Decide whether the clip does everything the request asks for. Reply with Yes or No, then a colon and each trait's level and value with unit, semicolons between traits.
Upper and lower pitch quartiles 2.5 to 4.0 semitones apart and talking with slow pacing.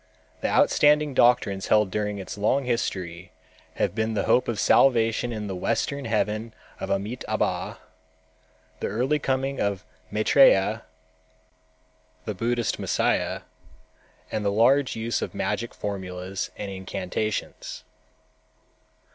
Yes: average, 3.6 semitones; slow, 115 wpm